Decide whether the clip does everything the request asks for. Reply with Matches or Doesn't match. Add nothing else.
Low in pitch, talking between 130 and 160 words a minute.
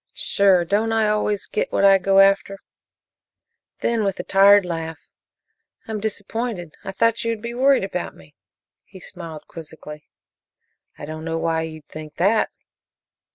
Doesn't match